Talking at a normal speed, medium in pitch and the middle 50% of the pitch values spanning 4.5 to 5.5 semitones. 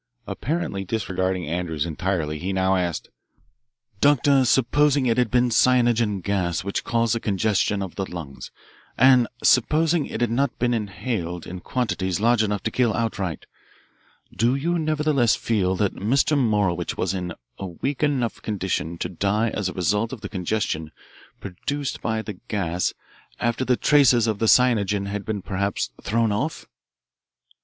No: average, 155 wpm; low, 105 Hz; average, 4.8 semitones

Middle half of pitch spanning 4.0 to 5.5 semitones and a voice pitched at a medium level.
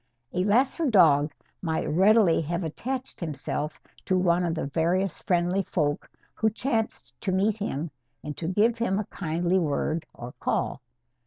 Yes: average, 4.5 semitones; medium, 180 Hz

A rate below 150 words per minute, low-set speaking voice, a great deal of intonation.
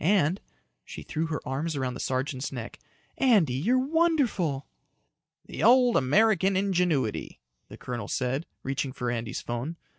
No: average, 140 wpm; medium, 150 Hz; wide, 7.4 semitones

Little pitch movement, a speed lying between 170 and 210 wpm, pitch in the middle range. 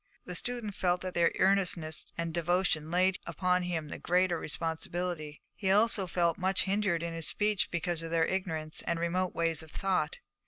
Yes: narrow, 2.2 semitones; average, 175 wpm; medium, 175 Hz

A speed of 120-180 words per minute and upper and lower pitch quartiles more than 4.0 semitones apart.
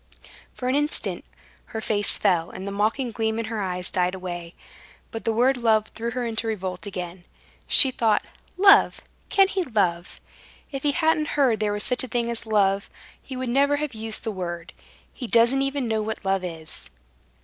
No: average, 190 wpm; average, 4.9 semitones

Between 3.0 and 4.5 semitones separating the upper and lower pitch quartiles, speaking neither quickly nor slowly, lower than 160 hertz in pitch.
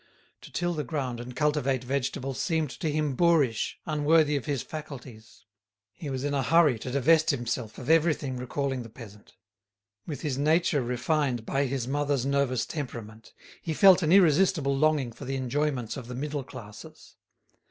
Yes: average, 3.5 semitones; average, 165 wpm; medium, 140 Hz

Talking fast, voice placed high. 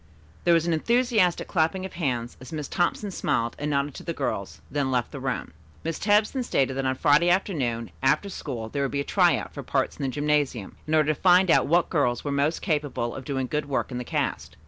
No: fast, 235 wpm; medium, 145 Hz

